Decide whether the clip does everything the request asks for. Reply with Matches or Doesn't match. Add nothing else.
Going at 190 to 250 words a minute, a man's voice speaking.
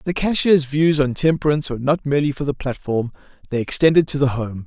Matches